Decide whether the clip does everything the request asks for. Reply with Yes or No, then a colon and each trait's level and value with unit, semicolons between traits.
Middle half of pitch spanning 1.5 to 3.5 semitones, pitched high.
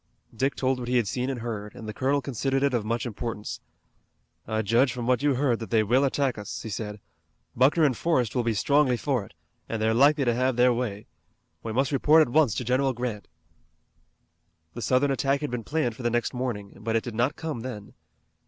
No: average, 3.2 semitones; low, 125 Hz